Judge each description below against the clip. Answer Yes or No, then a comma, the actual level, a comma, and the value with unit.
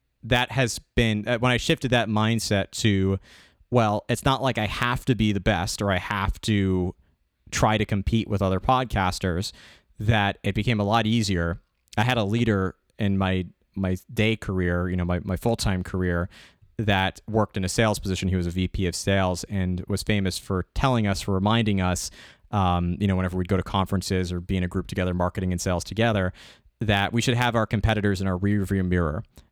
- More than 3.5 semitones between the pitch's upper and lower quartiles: No, average, 3.2 semitones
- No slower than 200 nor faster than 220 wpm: Yes, fast, 205 wpm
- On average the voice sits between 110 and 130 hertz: No, low, 100 Hz